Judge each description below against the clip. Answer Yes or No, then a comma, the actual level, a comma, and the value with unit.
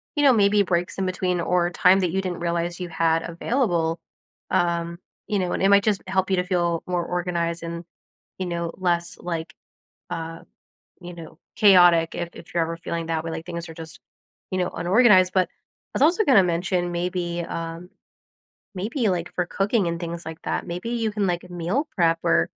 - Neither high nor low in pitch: Yes, medium, 175 Hz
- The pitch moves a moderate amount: No, narrow, 2.0 semitones